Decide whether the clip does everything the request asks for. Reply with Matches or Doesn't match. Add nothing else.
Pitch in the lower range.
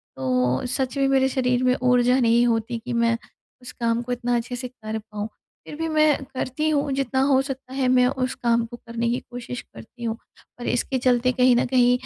Doesn't match